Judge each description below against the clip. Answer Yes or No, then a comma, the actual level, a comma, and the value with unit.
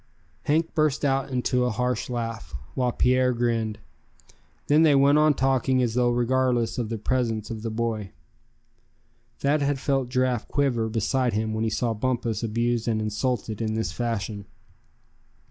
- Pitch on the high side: No, low, 120 Hz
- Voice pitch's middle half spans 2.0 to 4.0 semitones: Yes, narrow, 2.6 semitones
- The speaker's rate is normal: Yes, average, 160 wpm